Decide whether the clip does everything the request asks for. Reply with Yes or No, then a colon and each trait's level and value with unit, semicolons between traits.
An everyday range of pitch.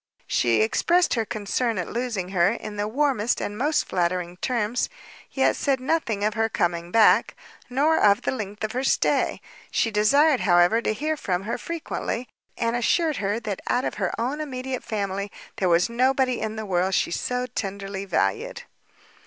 Yes: average, 4.6 semitones